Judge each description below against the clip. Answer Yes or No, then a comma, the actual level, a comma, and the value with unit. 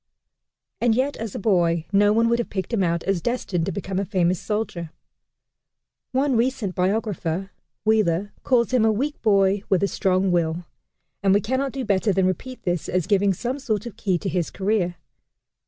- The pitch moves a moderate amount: Yes, average, 3.8 semitones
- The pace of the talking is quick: No, average, 190 wpm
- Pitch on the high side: Yes, high, 200 Hz